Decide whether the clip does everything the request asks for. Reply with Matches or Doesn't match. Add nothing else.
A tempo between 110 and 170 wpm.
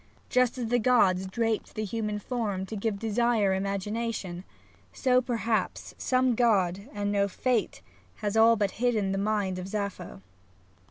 Matches